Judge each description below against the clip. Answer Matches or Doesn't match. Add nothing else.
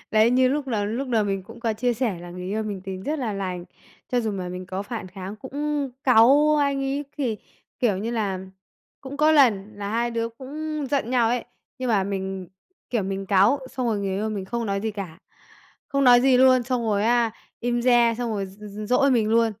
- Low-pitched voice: Doesn't match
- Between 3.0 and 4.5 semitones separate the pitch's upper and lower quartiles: Matches